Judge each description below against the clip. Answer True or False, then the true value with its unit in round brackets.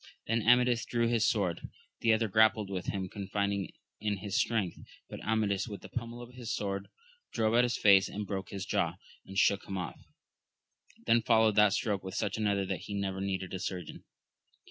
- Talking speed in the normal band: True (190 wpm)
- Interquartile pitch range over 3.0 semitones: False (2.7 semitones)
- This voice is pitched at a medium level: False (105 Hz)